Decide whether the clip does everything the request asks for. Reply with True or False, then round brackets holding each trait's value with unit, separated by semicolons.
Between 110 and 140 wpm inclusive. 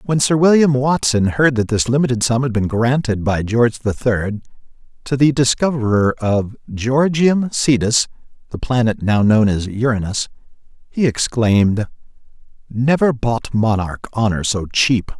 True (135 wpm)